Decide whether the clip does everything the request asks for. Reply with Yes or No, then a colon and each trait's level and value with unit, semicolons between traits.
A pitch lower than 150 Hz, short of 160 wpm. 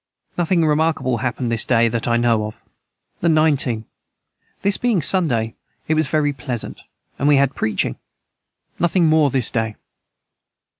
Yes: low, 135 Hz; average, 150 wpm